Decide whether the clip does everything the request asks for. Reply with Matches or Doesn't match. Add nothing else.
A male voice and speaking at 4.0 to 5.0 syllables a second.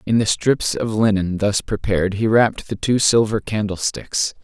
Matches